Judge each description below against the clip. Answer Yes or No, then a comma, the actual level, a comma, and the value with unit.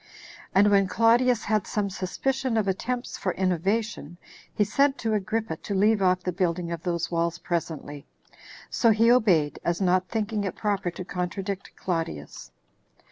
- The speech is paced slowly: No, average, 155 wpm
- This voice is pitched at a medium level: No, high, 195 Hz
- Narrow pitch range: No, average, 3.9 semitones